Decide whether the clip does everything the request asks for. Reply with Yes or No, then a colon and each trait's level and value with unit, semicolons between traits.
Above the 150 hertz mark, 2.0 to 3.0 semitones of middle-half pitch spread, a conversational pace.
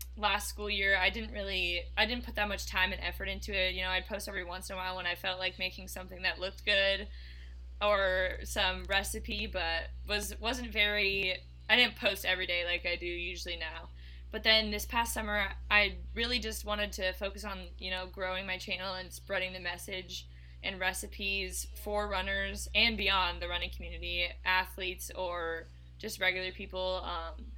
Yes: medium, 185 Hz; narrow, 2.6 semitones; average, 190 wpm